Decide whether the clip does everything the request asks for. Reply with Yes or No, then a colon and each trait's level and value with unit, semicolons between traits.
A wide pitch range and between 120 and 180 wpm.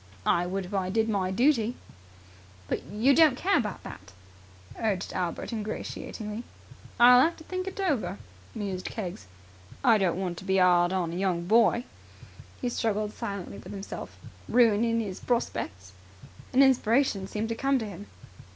No: average, 4.4 semitones; average, 160 wpm